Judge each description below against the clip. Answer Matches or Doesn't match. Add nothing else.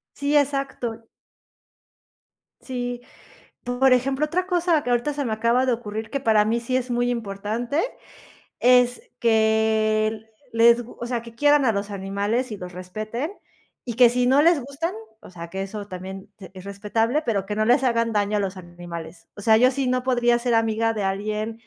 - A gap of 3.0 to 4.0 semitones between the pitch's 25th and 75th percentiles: Matches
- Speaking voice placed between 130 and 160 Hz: Doesn't match